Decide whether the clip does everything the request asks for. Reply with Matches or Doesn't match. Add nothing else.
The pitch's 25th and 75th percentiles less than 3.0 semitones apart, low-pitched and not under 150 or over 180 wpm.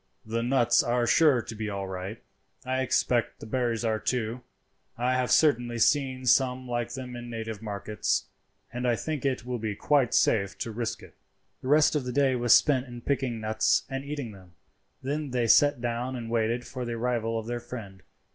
Doesn't match